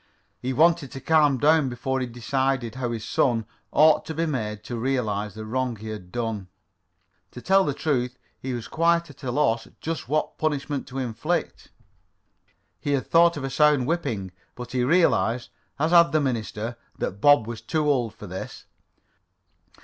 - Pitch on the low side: Yes, low, 130 Hz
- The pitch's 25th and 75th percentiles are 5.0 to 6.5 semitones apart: No, average, 4.6 semitones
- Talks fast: No, average, 175 wpm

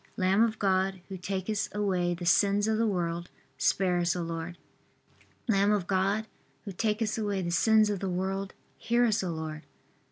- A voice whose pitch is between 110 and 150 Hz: No, high, 195 Hz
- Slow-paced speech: No, average, 180 wpm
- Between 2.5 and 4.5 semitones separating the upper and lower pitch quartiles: Yes, average, 2.9 semitones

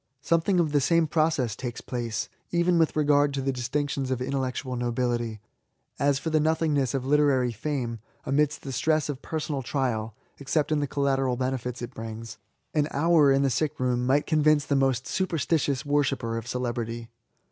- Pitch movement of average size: Yes, average, 3.2 semitones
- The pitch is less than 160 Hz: Yes, low, 135 Hz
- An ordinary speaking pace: Yes, average, 170 wpm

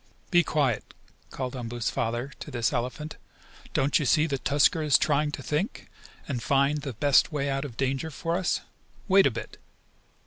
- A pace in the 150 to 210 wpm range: Yes, average, 175 wpm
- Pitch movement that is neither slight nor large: Yes, average, 3.0 semitones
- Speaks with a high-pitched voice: No, medium, 140 Hz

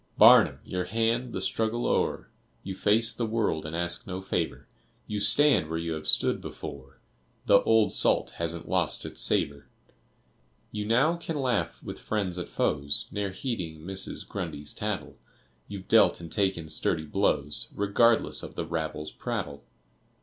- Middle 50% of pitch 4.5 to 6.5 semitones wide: Yes, wide, 5.6 semitones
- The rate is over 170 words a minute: No, average, 155 wpm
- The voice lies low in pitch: Yes, very low, 95 Hz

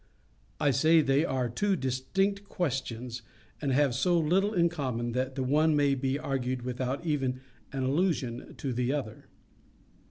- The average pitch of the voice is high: No, low, 135 Hz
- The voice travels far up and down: No, average, 3.7 semitones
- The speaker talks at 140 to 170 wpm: Yes, average, 155 wpm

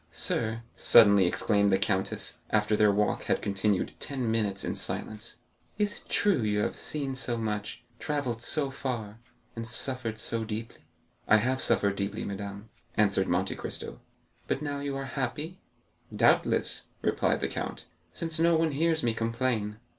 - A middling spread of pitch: Yes, average, 4.7 semitones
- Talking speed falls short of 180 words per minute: Yes, average, 160 wpm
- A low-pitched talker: Yes, low, 115 Hz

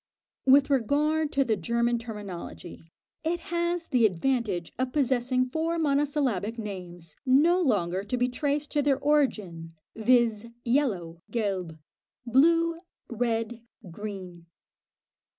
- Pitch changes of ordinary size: No, wide, 6.2 semitones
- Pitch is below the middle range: No, high, 240 Hz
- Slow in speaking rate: Yes, slow, 115 wpm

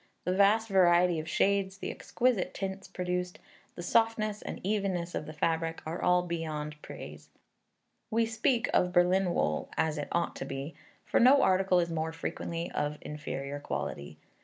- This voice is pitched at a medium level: Yes, medium, 180 Hz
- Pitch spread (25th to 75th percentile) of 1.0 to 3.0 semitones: No, average, 3.5 semitones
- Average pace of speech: Yes, average, 160 wpm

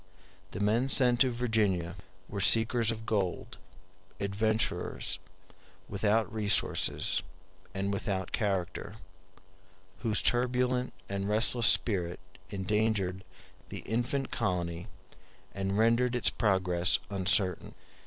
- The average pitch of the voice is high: No, low, 105 Hz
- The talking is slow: Yes, slow, 105 wpm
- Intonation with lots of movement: No, average, 3.3 semitones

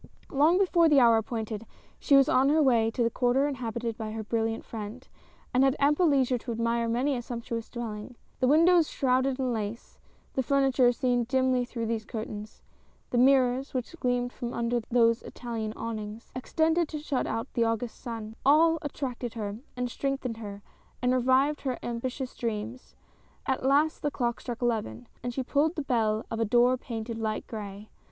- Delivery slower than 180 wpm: No, average, 185 wpm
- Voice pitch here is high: Yes, high, 245 Hz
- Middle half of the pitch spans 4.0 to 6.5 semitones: No, average, 2.9 semitones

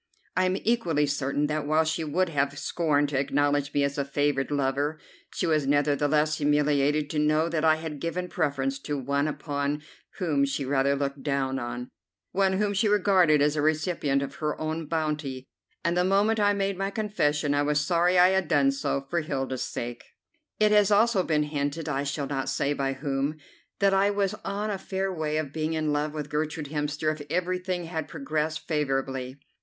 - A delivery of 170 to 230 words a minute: Yes, average, 190 wpm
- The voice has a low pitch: No, medium, 150 Hz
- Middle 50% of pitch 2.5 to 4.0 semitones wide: Yes, average, 3.5 semitones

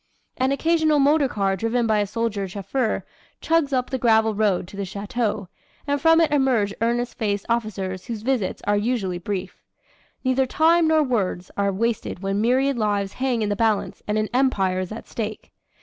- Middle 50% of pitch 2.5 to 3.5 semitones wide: No, average, 4.5 semitones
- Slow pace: No, average, 180 wpm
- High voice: Yes, high, 225 Hz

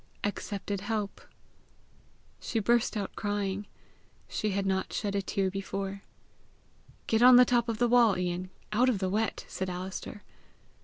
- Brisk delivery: No, average, 150 wpm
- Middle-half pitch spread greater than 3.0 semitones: No, average, 2.7 semitones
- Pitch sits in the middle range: No, high, 205 Hz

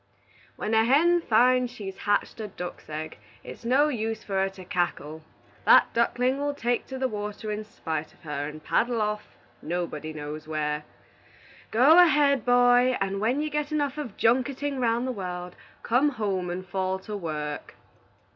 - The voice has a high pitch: Yes, high, 215 Hz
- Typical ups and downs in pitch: No, wide, 6.1 semitones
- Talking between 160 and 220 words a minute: Yes, average, 170 wpm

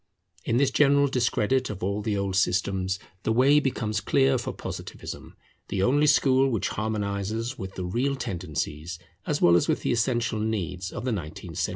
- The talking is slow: No, average, 180 wpm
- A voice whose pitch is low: Yes, low, 110 Hz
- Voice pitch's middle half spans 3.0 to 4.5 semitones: No, wide, 5.4 semitones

